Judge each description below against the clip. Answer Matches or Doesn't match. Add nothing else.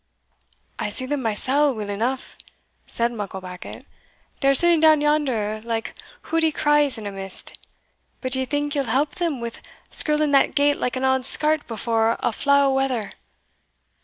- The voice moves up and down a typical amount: Matches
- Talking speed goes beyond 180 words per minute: Doesn't match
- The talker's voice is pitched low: Doesn't match